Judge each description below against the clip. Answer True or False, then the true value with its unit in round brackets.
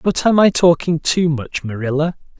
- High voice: False (160 Hz)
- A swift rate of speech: False (175 wpm)